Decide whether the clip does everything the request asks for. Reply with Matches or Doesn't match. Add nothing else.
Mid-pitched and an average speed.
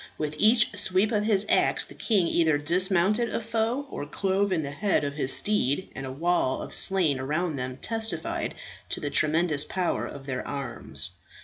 Matches